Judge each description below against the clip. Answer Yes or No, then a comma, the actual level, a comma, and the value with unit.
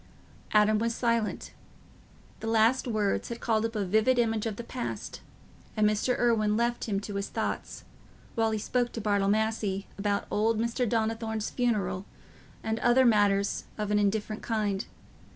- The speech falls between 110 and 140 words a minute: No, average, 160 wpm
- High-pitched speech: Yes, high, 220 Hz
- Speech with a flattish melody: Yes, narrow, 1.9 semitones